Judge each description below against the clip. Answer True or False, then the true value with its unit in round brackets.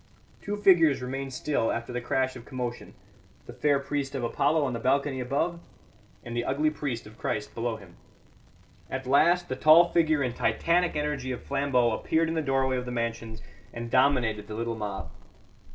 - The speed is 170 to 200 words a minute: True (185 wpm)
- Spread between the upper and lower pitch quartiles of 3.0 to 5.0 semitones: True (4.0 semitones)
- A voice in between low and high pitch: False (130 Hz)